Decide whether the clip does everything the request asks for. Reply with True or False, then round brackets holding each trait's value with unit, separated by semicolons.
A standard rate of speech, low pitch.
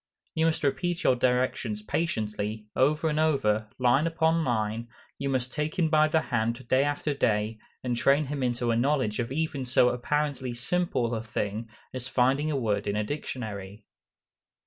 True (170 wpm; 130 Hz)